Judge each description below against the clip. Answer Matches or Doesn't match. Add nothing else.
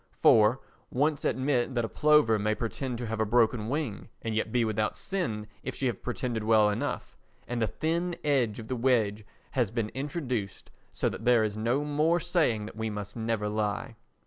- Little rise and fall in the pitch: Doesn't match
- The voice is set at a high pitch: Doesn't match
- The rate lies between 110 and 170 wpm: Doesn't match